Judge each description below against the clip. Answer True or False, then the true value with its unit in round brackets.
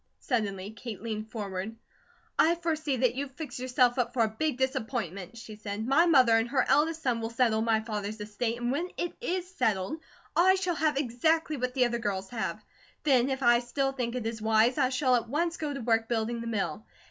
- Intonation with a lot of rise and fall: False (3.9 semitones)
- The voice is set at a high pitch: True (240 Hz)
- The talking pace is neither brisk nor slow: False (210 wpm)